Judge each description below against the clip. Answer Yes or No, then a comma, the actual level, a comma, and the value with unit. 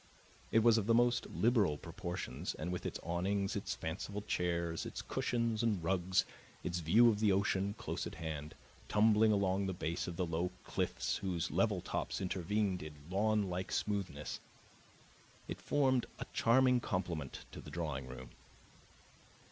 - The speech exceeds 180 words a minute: No, average, 155 wpm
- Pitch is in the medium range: No, very low, 95 Hz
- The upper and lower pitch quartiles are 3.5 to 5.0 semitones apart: Yes, average, 3.9 semitones